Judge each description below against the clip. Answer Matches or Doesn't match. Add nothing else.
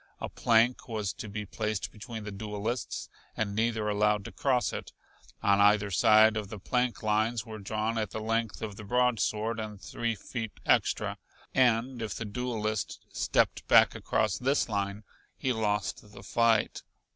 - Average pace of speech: Matches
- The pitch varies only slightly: Matches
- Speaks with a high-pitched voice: Doesn't match